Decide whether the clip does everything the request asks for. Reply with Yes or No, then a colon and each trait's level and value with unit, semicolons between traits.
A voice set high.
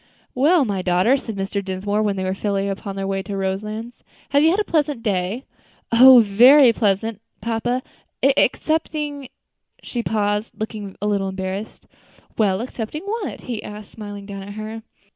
Yes: high, 215 Hz